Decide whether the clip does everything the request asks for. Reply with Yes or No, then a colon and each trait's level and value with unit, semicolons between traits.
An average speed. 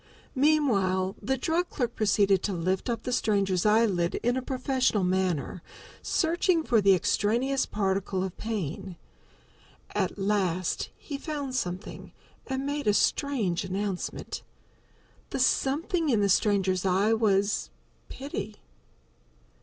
No: slow, 120 wpm